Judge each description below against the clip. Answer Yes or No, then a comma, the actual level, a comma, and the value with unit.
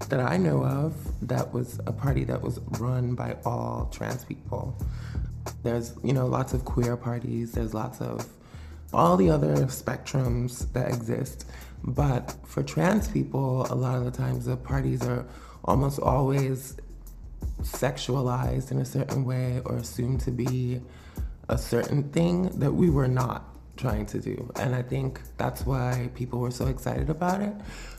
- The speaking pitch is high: No, low, 125 Hz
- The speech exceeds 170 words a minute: No, average, 160 wpm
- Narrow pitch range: Yes, narrow, 1.8 semitones